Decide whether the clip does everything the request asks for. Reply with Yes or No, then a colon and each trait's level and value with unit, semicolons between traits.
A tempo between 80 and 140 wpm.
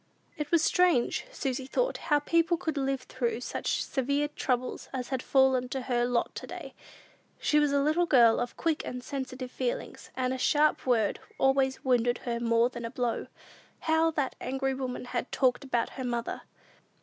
No: average, 180 wpm